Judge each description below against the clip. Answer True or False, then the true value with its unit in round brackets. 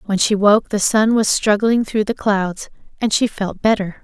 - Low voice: False (210 Hz)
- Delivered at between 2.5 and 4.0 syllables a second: False (4.5 syllables/s)